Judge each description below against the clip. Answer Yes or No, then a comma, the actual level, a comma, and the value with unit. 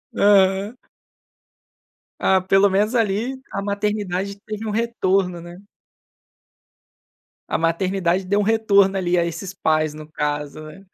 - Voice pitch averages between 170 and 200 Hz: Yes, high, 195 Hz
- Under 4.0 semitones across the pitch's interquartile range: Yes, average, 2.9 semitones